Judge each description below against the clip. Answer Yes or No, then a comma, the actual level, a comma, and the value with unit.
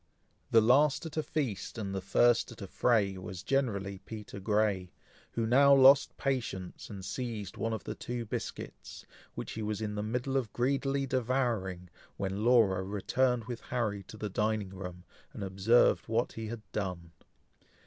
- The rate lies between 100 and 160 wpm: No, average, 170 wpm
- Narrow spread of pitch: No, average, 4.2 semitones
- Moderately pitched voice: No, low, 110 Hz